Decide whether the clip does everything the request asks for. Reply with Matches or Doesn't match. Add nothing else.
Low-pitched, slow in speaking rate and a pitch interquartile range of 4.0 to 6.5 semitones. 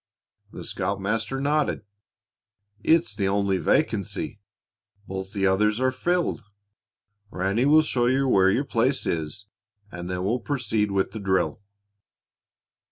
Matches